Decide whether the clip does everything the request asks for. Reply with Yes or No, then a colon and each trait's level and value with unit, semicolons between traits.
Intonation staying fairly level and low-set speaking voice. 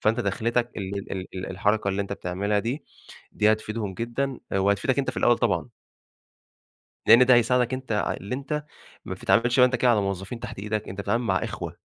No: average, 3.7 semitones; low, 110 Hz